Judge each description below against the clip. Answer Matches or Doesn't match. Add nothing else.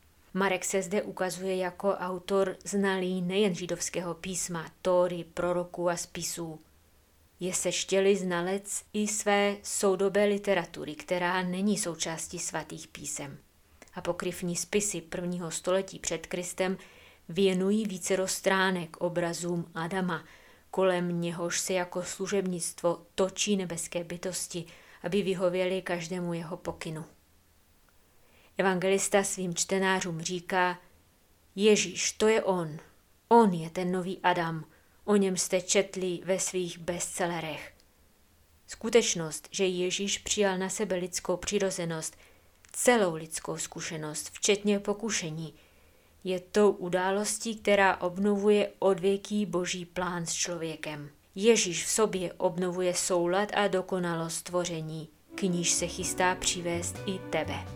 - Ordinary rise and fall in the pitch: Doesn't match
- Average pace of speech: Doesn't match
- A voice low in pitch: Doesn't match